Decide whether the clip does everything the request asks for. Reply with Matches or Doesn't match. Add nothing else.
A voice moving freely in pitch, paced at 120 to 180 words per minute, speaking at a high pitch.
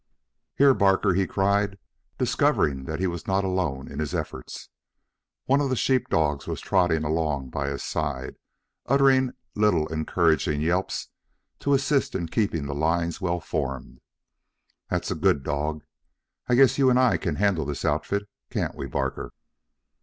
Doesn't match